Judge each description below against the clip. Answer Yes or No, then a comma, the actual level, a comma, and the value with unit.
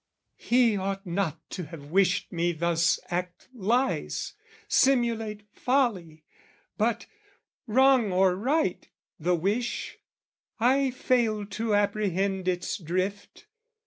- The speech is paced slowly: Yes, slow, 105 wpm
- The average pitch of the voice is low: No, high, 200 Hz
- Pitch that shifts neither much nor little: Yes, average, 4.7 semitones